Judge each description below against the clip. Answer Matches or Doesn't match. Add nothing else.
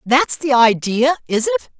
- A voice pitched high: Matches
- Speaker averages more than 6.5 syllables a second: Doesn't match